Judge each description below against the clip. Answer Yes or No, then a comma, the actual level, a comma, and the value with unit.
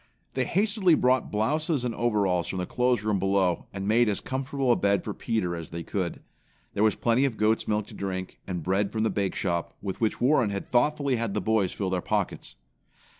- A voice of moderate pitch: No, low, 105 Hz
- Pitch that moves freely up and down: No, average, 4.4 semitones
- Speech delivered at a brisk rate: Yes, fast, 215 wpm